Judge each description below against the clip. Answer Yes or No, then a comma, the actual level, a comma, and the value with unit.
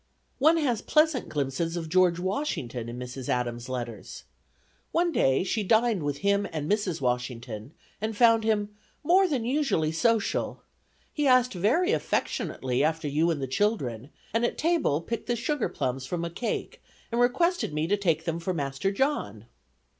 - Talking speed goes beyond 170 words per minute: No, average, 165 wpm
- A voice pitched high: No, medium, 180 Hz